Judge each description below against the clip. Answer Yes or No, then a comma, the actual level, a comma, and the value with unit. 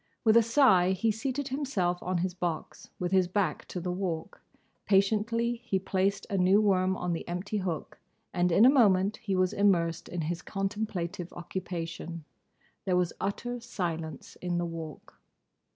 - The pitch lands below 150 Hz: No, medium, 185 Hz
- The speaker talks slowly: No, average, 165 wpm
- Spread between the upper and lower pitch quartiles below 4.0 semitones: Yes, average, 3.1 semitones